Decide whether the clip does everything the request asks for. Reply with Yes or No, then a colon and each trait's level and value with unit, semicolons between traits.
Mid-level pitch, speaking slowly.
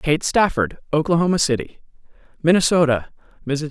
Yes: medium, 160 Hz; slow, 95 wpm